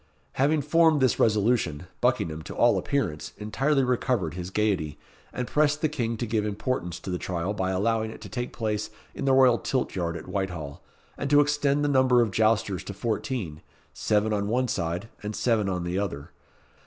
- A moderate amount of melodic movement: No, wide, 5.8 semitones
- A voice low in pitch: Yes, low, 110 Hz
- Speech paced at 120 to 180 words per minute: No, average, 190 wpm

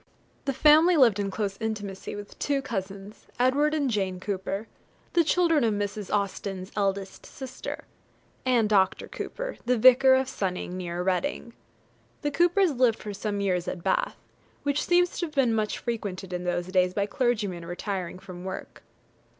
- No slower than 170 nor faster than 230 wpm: No, average, 160 wpm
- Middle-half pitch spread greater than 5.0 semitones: Yes, wide, 5.6 semitones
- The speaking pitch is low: No, high, 210 Hz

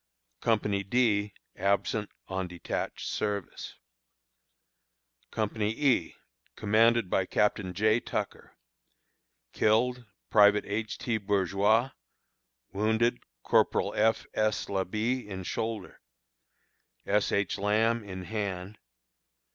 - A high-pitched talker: No, low, 105 Hz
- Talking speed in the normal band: No, slow, 90 wpm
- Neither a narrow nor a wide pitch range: No, narrow, 2.2 semitones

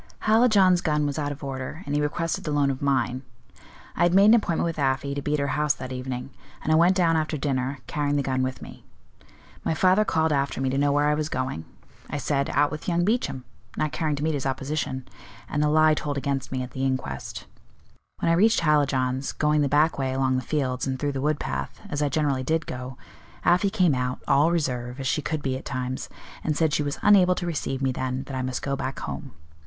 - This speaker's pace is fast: Yes, fast, 235 wpm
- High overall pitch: No, medium, 145 Hz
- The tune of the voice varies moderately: Yes, average, 3.1 semitones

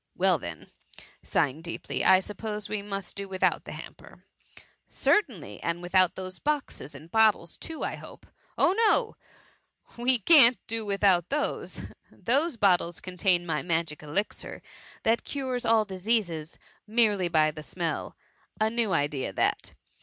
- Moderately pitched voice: No, high, 195 Hz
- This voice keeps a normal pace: Yes, average, 160 wpm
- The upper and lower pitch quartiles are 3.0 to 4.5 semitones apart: No, average, 5.1 semitones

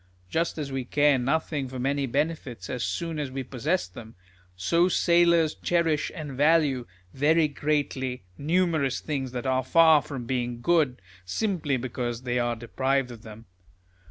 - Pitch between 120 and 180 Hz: Yes, low, 135 Hz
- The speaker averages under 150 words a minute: No, average, 155 wpm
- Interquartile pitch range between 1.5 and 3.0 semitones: No, average, 4.3 semitones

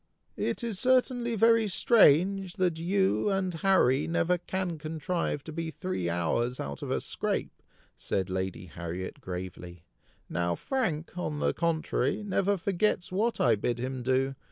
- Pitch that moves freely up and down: Yes, wide, 8.3 semitones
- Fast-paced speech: No, average, 150 wpm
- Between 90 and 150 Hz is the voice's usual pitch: No, medium, 165 Hz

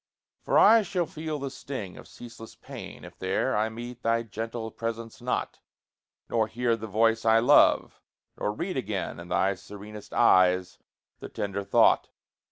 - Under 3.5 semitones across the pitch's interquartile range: Yes, average, 2.8 semitones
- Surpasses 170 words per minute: No, average, 160 wpm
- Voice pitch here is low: Yes, low, 115 Hz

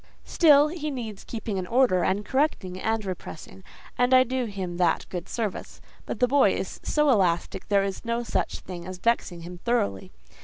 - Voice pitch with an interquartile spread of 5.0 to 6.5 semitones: Yes, wide, 5.5 semitones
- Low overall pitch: No, high, 210 Hz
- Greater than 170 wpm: Yes, average, 185 wpm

